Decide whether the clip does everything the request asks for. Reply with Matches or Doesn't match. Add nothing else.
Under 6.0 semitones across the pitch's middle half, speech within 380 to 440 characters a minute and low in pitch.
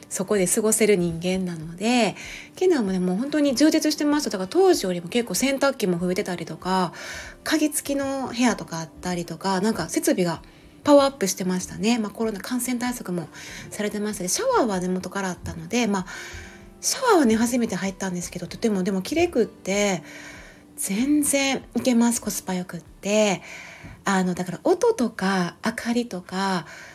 Doesn't match